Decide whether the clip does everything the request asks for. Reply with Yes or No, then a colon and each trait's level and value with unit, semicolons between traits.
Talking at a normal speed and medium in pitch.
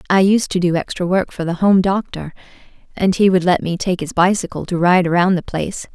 No: fast, 230 wpm; medium, 180 Hz